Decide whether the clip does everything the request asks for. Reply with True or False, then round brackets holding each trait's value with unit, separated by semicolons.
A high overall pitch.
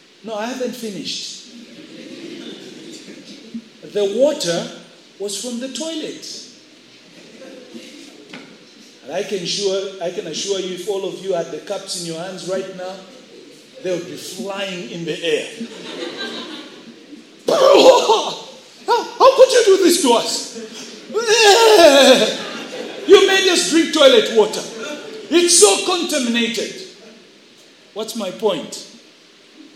True (260 Hz)